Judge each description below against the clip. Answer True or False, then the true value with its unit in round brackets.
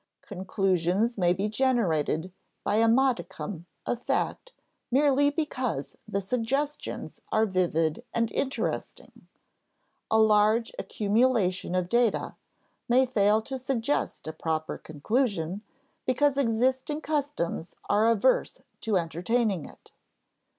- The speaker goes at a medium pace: False (110 wpm)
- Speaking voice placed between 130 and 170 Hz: False (220 Hz)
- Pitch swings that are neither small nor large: False (5.8 semitones)